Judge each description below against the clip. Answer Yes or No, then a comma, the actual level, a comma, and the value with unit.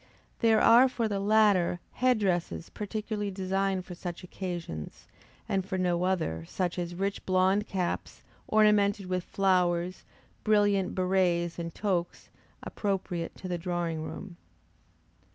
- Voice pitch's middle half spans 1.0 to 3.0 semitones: Yes, narrow, 2.6 semitones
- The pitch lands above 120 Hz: Yes, medium, 185 Hz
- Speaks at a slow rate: Yes, slow, 130 wpm